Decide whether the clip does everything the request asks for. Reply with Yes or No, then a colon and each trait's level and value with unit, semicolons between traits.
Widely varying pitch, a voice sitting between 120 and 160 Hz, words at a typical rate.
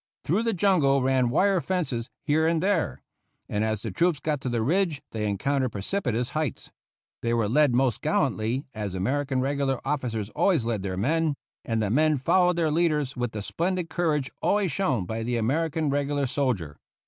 Yes: wide, 5.7 semitones; medium, 140 Hz; average, 180 wpm